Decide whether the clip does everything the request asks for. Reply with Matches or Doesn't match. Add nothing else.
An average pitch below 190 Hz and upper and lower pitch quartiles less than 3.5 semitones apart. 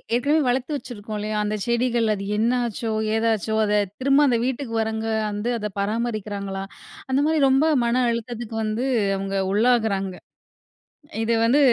Doesn't match